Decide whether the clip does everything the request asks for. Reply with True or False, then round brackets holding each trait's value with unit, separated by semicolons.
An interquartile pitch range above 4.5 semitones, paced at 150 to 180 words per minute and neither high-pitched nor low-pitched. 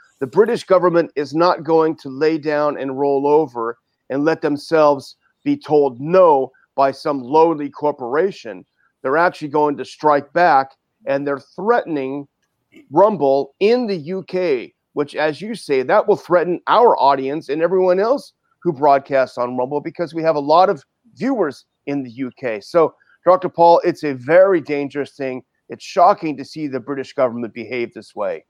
False (4.2 semitones; 165 wpm; 150 Hz)